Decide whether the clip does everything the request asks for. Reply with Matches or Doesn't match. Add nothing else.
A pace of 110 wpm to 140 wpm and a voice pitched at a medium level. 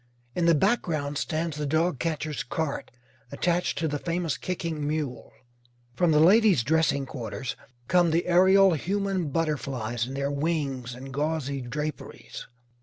Matches